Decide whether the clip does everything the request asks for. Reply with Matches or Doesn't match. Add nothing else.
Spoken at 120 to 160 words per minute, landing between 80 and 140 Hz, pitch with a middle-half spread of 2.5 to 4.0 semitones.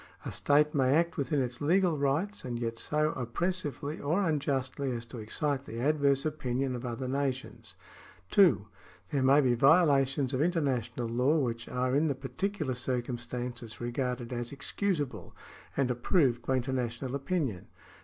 Matches